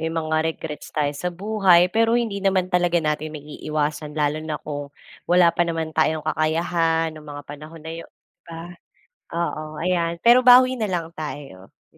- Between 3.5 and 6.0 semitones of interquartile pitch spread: No, narrow, 2.6 semitones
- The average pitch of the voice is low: No, medium, 165 Hz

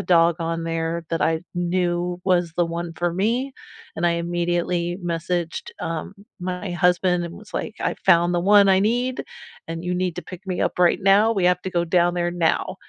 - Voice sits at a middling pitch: Yes, medium, 175 Hz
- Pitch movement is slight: Yes, narrow, 1.4 semitones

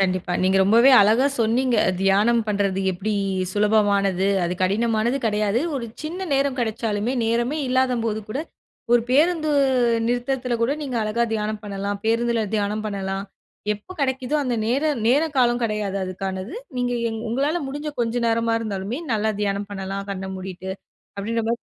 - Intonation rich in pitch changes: No, average, 3.6 semitones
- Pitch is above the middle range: Yes, high, 220 Hz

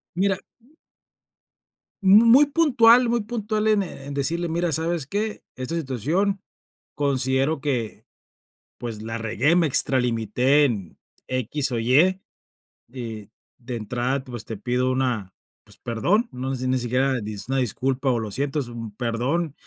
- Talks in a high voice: No, low, 135 Hz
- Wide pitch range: Yes, wide, 6.2 semitones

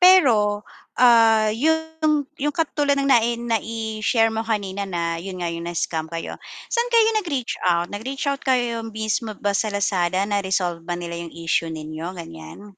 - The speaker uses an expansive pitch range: Yes, wide, 6.2 semitones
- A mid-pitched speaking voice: No, high, 215 Hz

